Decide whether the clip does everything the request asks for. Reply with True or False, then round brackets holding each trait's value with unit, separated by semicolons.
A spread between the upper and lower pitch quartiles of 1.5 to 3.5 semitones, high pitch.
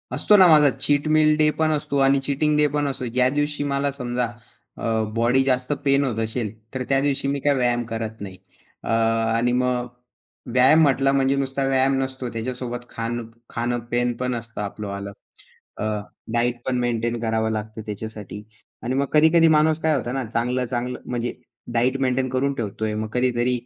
False (2.9 semitones; 125 Hz)